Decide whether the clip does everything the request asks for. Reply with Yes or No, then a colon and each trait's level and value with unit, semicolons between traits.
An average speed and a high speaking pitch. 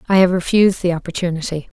No: average, 170 wpm; medium, 175 Hz